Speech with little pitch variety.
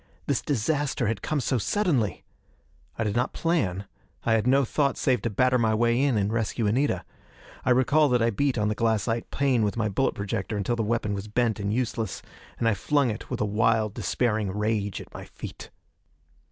No: average, 3.4 semitones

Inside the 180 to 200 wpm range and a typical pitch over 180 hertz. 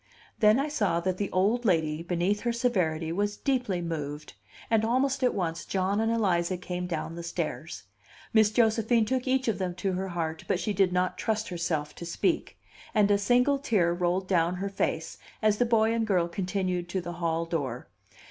Yes: average, 195 wpm; high, 190 Hz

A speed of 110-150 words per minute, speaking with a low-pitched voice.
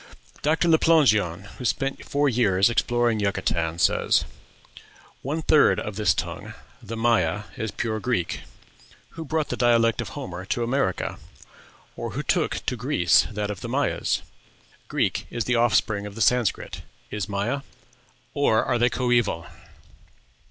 Yes: average, 145 wpm; low, 115 Hz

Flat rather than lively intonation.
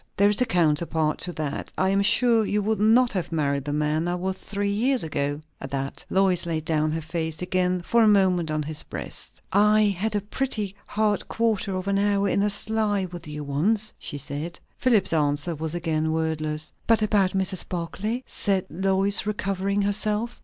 No: average, 4.5 semitones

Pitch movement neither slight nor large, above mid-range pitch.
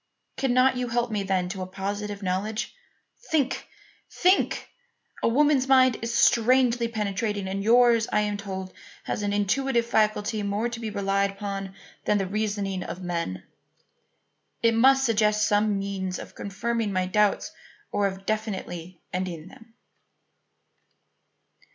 Yes: average, 3.1 semitones; high, 210 Hz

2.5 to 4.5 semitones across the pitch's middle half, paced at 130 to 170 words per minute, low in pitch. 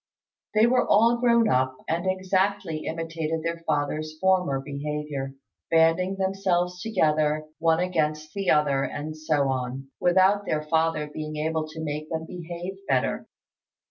No: average, 3.4 semitones; average, 140 wpm; medium, 160 Hz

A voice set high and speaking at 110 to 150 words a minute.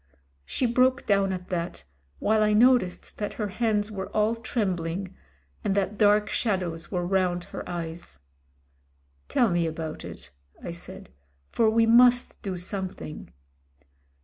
Yes: high, 200 Hz; average, 145 wpm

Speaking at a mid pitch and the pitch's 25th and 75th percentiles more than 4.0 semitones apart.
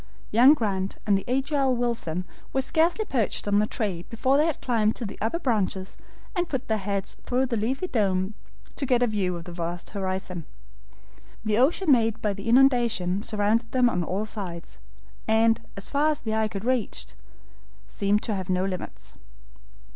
No: high, 220 Hz; average, 4.7 semitones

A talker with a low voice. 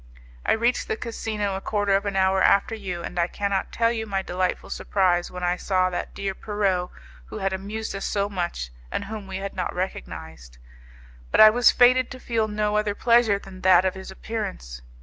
No: high, 195 Hz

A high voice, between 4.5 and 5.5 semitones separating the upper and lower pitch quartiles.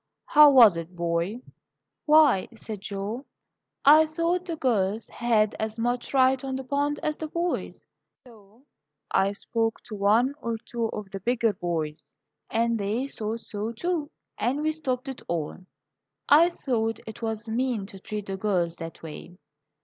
Yes: high, 230 Hz; average, 5.0 semitones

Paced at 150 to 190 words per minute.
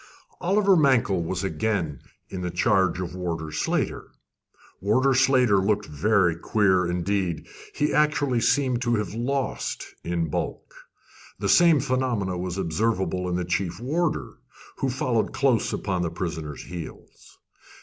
No: slow, 135 wpm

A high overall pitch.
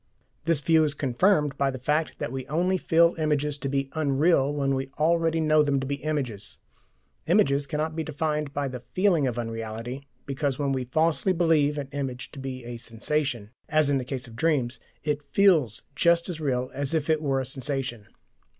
No: medium, 140 Hz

